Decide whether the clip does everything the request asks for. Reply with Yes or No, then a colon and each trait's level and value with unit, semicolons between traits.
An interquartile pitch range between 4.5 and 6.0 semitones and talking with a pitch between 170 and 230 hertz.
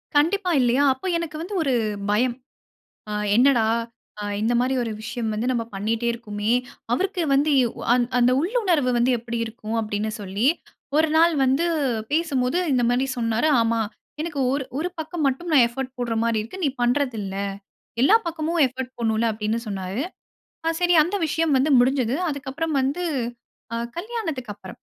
No: average, 5.3 semitones; very high, 255 Hz